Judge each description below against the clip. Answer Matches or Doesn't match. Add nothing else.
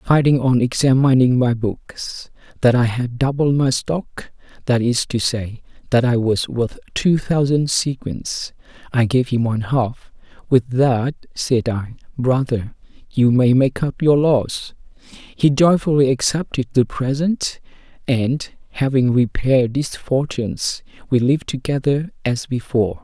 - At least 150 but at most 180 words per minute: Doesn't match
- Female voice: Doesn't match